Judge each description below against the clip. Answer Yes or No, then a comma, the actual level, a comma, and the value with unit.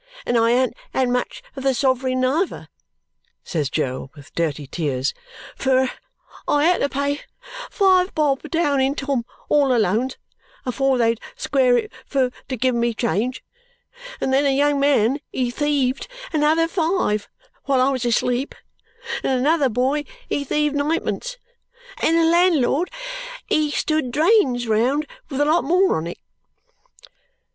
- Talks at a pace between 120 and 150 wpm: Yes, average, 145 wpm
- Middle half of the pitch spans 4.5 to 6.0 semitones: No, average, 3.5 semitones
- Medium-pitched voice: No, very high, 270 Hz